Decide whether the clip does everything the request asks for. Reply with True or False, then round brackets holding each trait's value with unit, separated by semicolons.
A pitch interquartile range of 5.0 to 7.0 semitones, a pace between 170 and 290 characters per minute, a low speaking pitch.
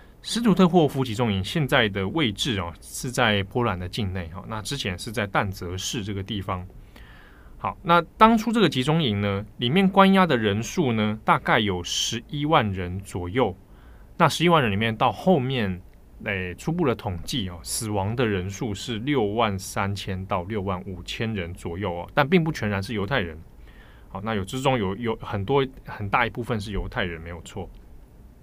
True (5.3 semitones; 280 characters per minute; 105 Hz)